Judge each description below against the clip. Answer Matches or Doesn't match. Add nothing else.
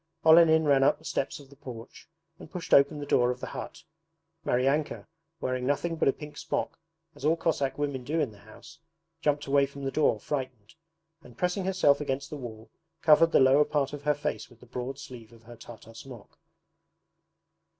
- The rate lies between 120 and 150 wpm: Doesn't match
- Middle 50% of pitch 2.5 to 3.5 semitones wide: Matches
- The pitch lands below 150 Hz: Matches